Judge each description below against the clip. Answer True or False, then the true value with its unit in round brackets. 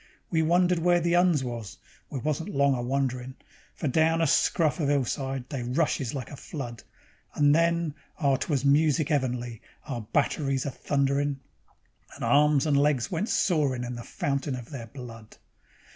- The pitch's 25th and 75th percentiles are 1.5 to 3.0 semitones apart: False (3.5 semitones)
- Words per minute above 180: False (165 wpm)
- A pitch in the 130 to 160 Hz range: True (140 Hz)